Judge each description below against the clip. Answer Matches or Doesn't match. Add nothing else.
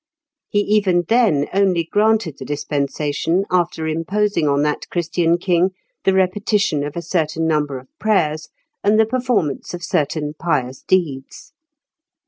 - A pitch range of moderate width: Matches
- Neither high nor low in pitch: Matches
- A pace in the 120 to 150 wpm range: Matches